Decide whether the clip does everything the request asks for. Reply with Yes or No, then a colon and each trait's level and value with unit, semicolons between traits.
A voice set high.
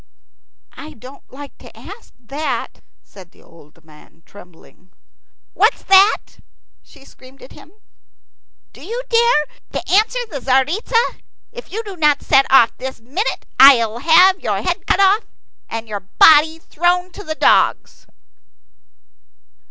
Yes: very high, 295 Hz